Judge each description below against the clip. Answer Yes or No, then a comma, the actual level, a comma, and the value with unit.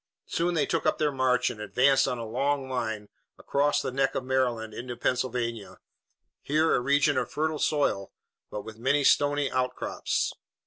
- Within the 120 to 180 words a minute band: Yes, average, 170 wpm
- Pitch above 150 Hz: No, low, 130 Hz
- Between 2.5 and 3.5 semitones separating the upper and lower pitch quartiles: Yes, average, 3.1 semitones